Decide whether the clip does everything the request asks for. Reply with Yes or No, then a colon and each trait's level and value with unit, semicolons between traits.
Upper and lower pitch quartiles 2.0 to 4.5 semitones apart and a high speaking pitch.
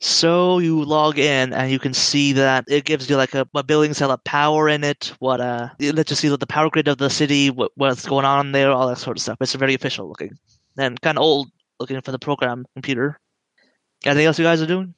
No: narrow, 2.4 semitones; medium, 140 Hz